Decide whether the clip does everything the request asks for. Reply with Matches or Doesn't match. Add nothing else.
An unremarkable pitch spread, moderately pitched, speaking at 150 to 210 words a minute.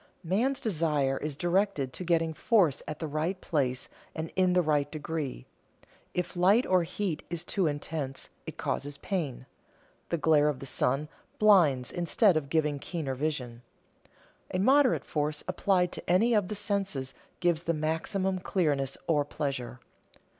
Matches